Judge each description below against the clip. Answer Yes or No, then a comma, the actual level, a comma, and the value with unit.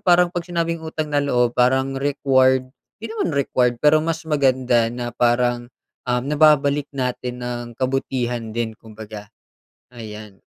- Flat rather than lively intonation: No, average, 3.3 semitones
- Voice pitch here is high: No, low, 130 Hz